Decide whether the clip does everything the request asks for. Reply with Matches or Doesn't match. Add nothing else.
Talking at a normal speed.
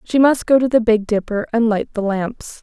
Doesn't match